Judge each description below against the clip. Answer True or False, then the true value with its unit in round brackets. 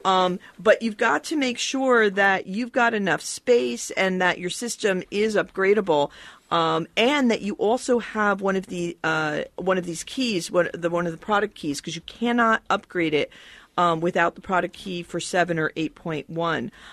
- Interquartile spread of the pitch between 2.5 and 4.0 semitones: False (4.4 semitones)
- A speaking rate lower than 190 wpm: False (200 wpm)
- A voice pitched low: False (190 Hz)